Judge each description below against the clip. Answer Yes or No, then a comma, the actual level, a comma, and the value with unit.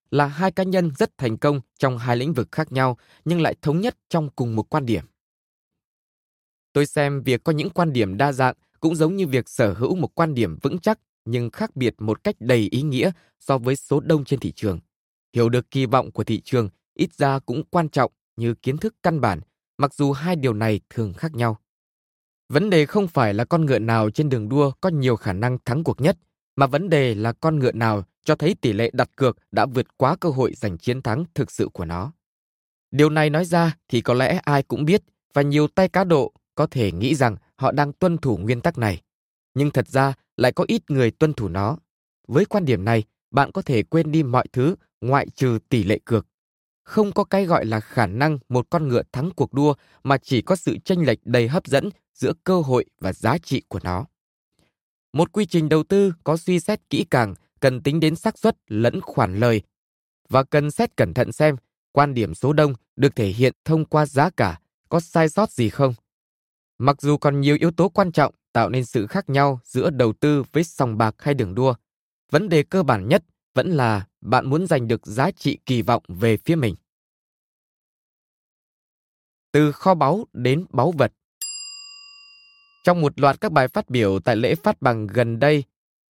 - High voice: No, medium, 140 Hz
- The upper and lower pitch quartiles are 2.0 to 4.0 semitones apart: No, average, 5.3 semitones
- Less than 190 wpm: No, average, 215 wpm